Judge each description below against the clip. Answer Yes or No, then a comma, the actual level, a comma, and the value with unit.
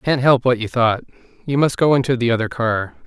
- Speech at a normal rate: No, fast, 215 wpm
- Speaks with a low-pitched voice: Yes, low, 125 Hz